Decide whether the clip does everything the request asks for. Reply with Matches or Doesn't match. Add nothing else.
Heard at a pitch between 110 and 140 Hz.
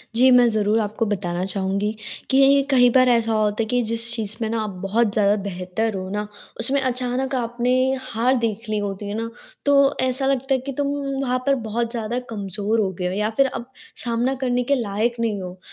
Doesn't match